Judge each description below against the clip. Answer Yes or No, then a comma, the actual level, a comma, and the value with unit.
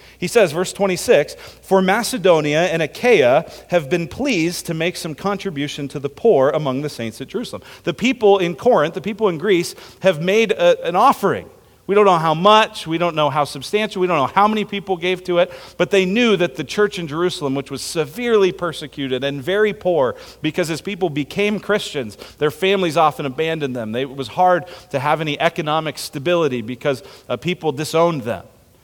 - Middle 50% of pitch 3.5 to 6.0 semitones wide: Yes, average, 4.8 semitones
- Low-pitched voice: No, medium, 175 Hz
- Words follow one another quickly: No, average, 190 wpm